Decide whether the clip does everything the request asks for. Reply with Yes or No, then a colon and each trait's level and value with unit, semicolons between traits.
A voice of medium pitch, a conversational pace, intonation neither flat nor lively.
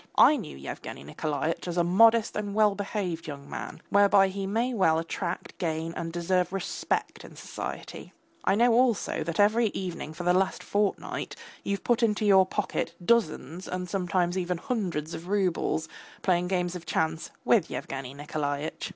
Yes: medium, 180 Hz; average, 165 wpm; average, 3.8 semitones